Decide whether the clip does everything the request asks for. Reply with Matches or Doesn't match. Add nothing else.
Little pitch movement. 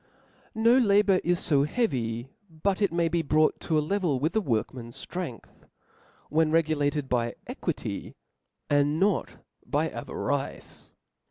Doesn't match